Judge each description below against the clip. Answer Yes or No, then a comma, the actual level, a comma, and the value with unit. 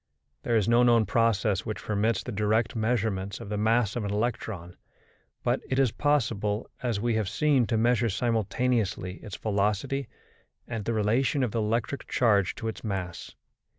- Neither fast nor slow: Yes, average, 170 wpm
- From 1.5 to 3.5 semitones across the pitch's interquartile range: Yes, average, 2.7 semitones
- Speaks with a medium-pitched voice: No, low, 110 Hz